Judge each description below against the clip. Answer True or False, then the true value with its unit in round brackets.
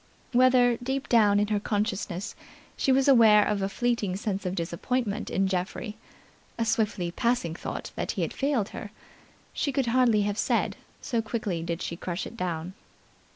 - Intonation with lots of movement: False (4.2 semitones)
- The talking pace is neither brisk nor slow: True (170 wpm)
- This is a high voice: True (210 Hz)